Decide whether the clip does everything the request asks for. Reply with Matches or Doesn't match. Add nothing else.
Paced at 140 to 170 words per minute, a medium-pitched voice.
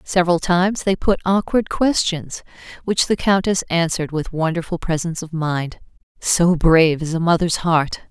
Matches